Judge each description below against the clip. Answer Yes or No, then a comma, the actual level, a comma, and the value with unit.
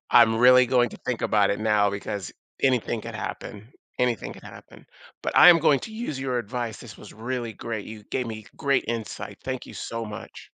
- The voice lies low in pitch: Yes, low, 115 Hz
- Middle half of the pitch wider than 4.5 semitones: No, average, 2.8 semitones